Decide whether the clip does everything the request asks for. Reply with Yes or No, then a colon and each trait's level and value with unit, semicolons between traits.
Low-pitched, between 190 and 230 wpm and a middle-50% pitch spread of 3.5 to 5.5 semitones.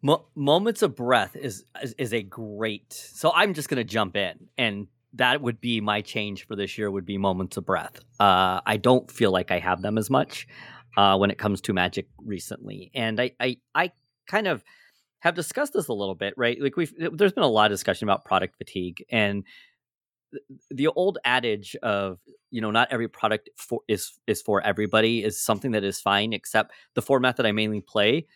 Yes: low, 110 Hz; fast, 205 wpm; average, 4.0 semitones